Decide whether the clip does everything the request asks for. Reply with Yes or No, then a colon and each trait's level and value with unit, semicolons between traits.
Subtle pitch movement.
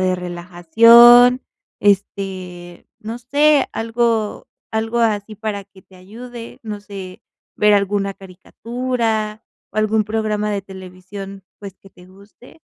No: average, 3.0 semitones